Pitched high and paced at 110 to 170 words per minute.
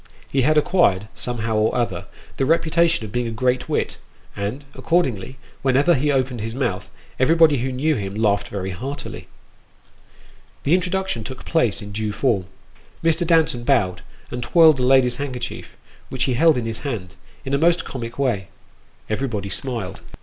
No: low, 125 Hz; average, 165 wpm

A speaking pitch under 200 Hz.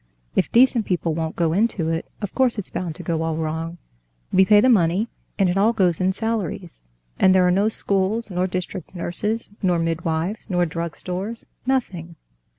Yes: medium, 185 Hz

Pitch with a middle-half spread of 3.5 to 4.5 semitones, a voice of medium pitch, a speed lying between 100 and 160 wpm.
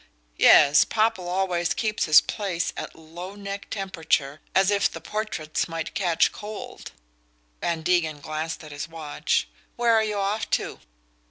Yes: average, 4.2 semitones; medium, 180 Hz; average, 150 wpm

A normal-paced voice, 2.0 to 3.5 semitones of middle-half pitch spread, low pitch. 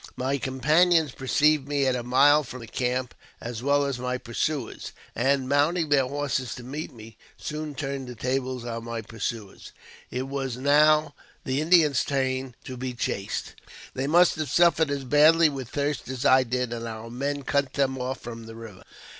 Yes: average, 180 wpm; average, 2.8 semitones; low, 130 Hz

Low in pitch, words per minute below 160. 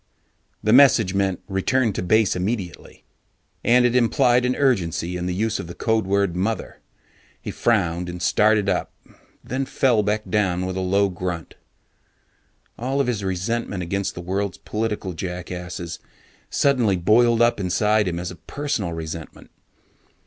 Yes: low, 100 Hz; average, 150 wpm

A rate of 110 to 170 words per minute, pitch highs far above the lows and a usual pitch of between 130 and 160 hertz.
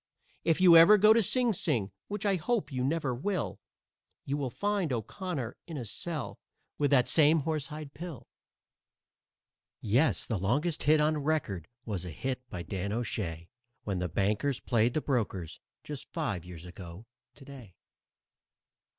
Yes: average, 150 wpm; wide, 7.5 semitones; low, 135 Hz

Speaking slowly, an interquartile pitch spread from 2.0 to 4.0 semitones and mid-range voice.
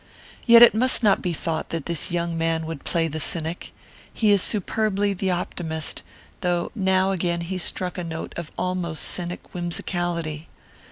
No: average, 165 wpm; narrow, 2.5 semitones; medium, 175 Hz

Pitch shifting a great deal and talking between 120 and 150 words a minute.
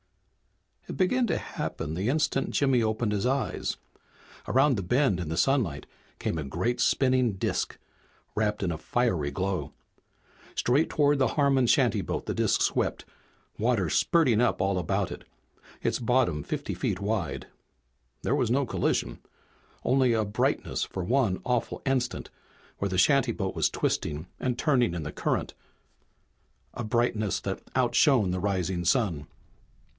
Yes: wide, 5.9 semitones; average, 145 wpm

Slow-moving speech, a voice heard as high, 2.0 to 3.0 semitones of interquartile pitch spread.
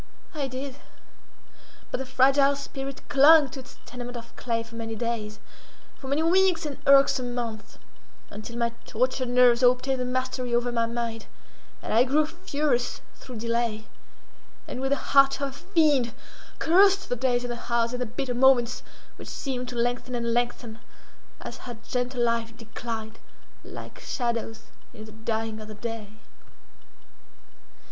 No: average, 155 wpm; high, 245 Hz; narrow, 2.6 semitones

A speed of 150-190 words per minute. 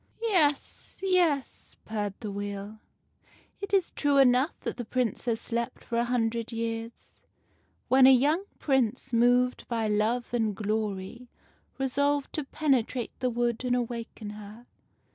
No: slow, 135 wpm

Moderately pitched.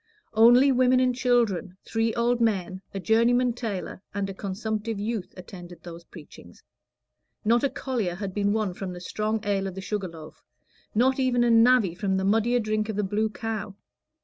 No: high, 215 Hz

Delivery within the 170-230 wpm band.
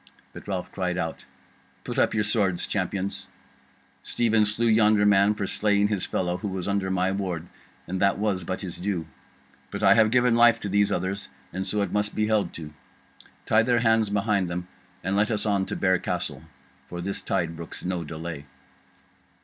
Yes: average, 190 wpm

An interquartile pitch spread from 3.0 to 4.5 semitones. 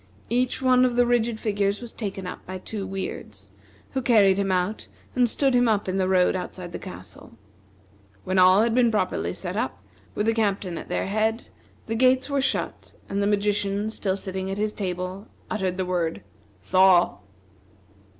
Yes: average, 3.4 semitones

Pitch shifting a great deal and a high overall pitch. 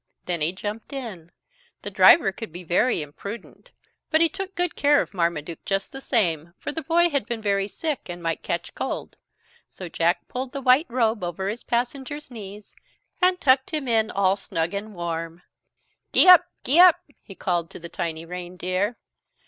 Yes: wide, 7.6 semitones; high, 205 Hz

